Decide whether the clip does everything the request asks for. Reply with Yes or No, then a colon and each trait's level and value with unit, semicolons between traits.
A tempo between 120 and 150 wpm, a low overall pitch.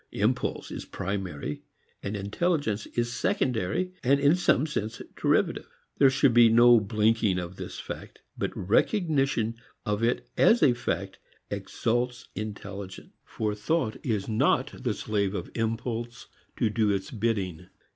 Yes: slow, 135 wpm; low, 115 Hz